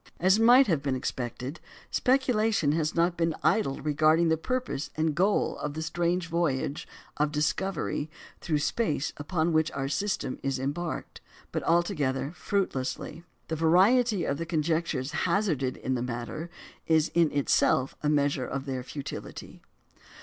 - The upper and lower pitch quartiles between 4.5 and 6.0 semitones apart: No, average, 3.7 semitones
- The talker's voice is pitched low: No, medium, 160 Hz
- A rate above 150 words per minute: No, average, 145 wpm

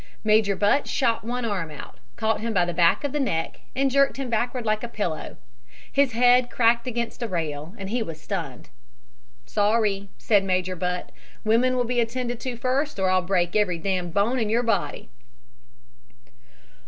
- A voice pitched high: Yes, high, 220 Hz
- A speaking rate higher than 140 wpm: Yes, average, 180 wpm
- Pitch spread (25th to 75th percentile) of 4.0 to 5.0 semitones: Yes, average, 4.7 semitones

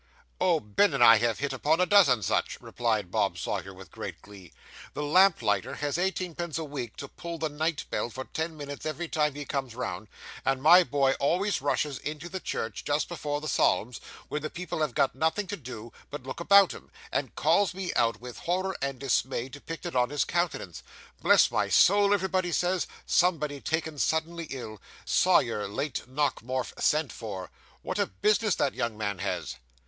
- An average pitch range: No, wide, 5.8 semitones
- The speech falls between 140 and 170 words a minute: No, average, 185 wpm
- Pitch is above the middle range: No, medium, 145 Hz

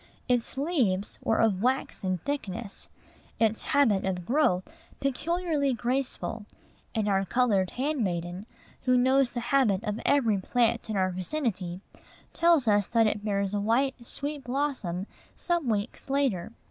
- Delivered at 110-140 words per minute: Yes, slow, 135 wpm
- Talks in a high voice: Yes, high, 230 Hz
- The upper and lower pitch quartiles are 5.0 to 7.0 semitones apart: Yes, wide, 5.6 semitones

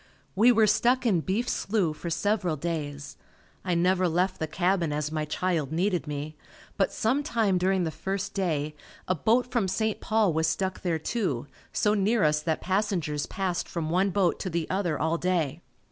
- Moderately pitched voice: Yes, medium, 180 Hz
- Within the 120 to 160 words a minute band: No, average, 185 wpm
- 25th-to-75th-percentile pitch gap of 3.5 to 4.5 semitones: Yes, average, 4.2 semitones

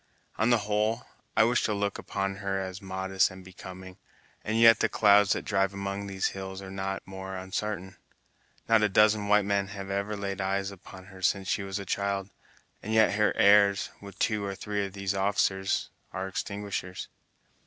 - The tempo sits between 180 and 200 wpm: Yes, average, 185 wpm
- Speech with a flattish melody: Yes, narrow, 1.3 semitones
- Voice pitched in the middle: No, low, 100 Hz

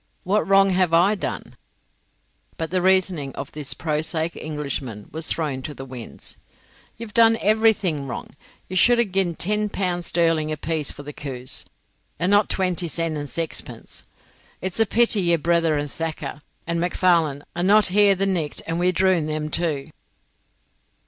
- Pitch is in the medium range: Yes, medium, 170 Hz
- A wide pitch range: No, average, 3.9 semitones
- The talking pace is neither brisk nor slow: Yes, average, 160 wpm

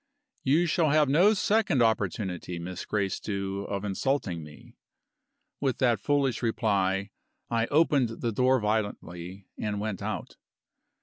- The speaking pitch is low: Yes, low, 110 Hz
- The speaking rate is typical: No, slow, 125 wpm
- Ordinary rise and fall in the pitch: No, wide, 5.7 semitones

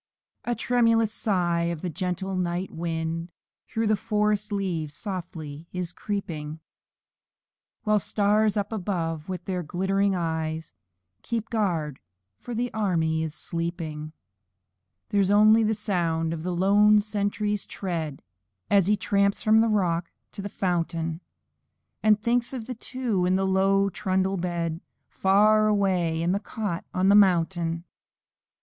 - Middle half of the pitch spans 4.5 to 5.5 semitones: No, average, 3.8 semitones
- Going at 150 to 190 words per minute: No, average, 140 wpm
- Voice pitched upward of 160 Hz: Yes, high, 190 Hz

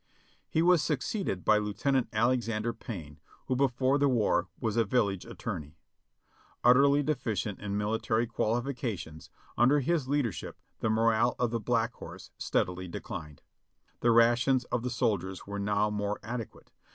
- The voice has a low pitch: Yes, low, 115 Hz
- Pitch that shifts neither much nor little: Yes, average, 3.6 semitones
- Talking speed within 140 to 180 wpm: Yes, average, 145 wpm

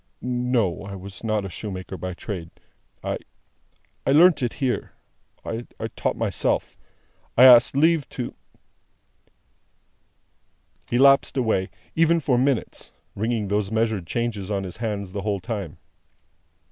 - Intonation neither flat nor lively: Yes, average, 4.3 semitones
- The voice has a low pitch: Yes, low, 110 Hz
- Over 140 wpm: No, slow, 135 wpm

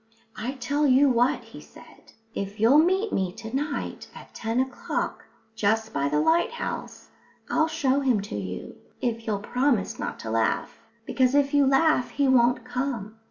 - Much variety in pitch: No, average, 4.3 semitones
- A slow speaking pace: No, average, 165 wpm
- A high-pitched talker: Yes, very high, 250 Hz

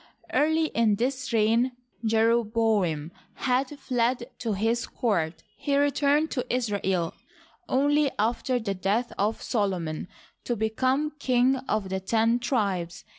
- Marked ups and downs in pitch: No, average, 4.2 semitones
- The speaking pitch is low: No, high, 230 Hz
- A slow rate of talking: Yes, slow, 125 wpm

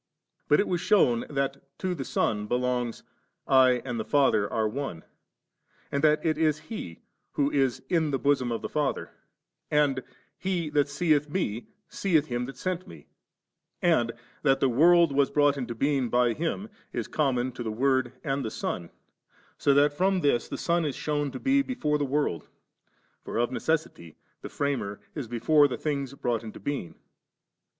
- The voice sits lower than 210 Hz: Yes, medium, 140 Hz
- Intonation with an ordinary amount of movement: Yes, average, 3.8 semitones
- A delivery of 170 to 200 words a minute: Yes, average, 180 wpm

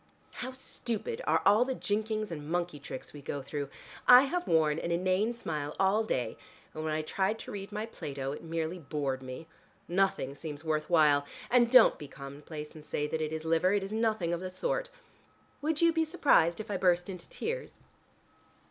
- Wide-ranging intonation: Yes, wide, 6.4 semitones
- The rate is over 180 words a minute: Yes, average, 195 wpm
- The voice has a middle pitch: Yes, medium, 175 Hz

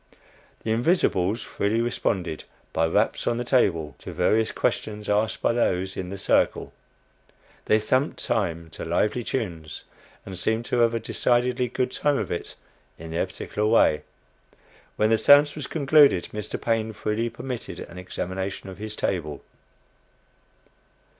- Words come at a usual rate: Yes, average, 145 wpm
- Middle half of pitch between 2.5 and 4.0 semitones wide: No, average, 4.5 semitones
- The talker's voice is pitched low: Yes, low, 110 Hz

